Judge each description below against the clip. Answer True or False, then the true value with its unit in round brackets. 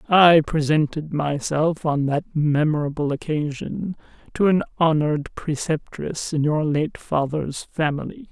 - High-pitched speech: False (155 Hz)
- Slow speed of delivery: True (115 wpm)